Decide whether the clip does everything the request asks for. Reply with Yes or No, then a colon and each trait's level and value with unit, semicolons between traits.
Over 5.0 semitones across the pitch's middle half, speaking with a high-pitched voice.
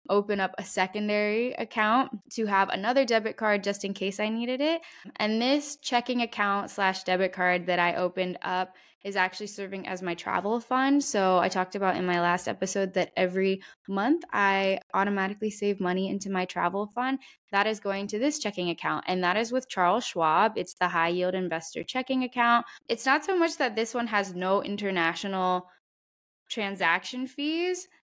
No: average, 4.3 semitones; high, 200 Hz